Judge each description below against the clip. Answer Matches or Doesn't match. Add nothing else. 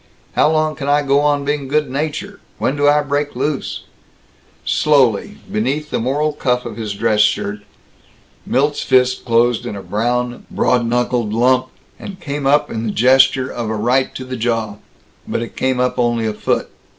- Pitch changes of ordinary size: Matches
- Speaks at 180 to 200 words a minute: Matches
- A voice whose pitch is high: Doesn't match